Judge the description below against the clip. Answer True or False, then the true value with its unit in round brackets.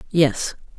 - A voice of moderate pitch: True (150 Hz)